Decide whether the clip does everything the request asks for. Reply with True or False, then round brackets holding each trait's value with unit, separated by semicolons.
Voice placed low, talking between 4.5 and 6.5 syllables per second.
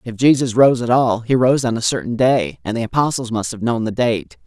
True (125 Hz; 5.4 syllables/s)